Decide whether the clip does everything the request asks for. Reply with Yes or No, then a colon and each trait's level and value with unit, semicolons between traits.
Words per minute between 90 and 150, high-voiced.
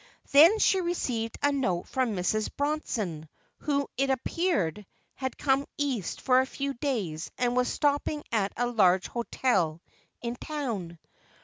Yes: average, 140 wpm; very high, 250 Hz